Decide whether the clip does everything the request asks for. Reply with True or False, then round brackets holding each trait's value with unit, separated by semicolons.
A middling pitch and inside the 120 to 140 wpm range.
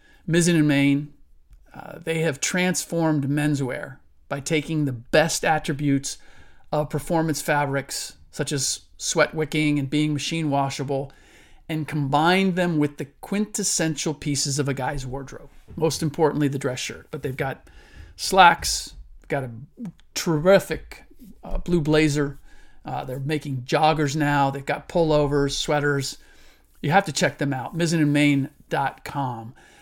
True (150 Hz; 135 wpm)